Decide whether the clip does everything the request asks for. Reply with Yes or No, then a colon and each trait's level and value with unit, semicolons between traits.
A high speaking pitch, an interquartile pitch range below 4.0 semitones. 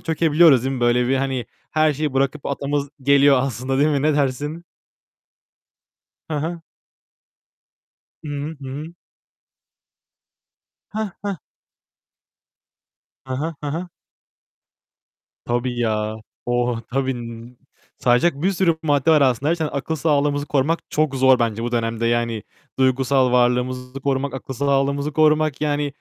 No: medium, 140 Hz; average, 3.2 semitones